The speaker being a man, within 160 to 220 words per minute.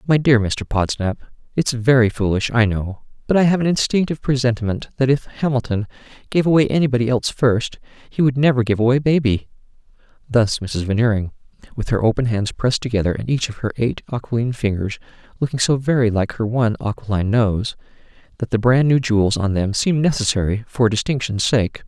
Yes: male; average, 180 wpm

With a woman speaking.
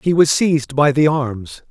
No: male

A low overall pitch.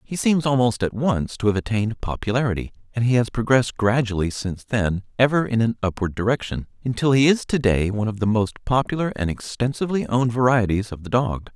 Yes: low, 115 Hz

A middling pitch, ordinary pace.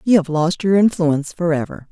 Yes: medium, 170 Hz; average, 190 wpm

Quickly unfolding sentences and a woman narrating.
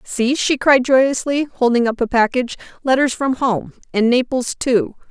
No: average, 165 wpm; female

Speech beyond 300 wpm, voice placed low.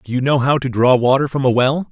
Yes: fast, 315 wpm; low, 130 Hz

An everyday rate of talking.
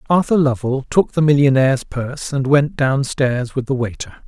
Yes: average, 185 wpm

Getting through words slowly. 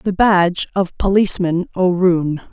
Yes: slow, 120 wpm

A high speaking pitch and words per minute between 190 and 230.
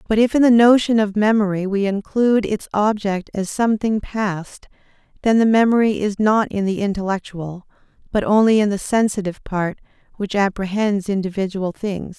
No: high, 205 Hz; average, 160 wpm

